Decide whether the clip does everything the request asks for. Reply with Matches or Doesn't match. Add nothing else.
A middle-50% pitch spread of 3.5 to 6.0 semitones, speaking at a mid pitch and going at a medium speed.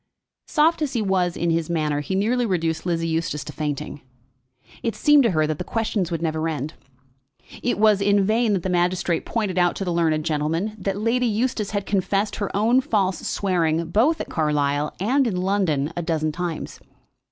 Matches